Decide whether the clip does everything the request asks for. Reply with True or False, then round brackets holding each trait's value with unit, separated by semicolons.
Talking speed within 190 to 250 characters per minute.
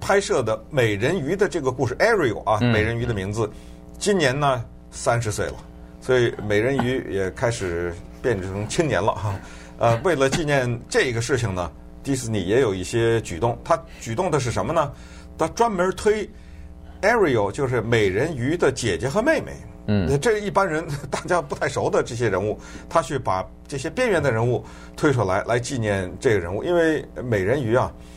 False (285 characters per minute)